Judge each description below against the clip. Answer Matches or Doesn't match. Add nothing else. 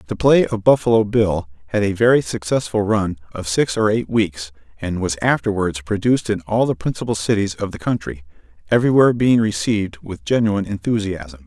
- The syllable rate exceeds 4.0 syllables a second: Matches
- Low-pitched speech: Matches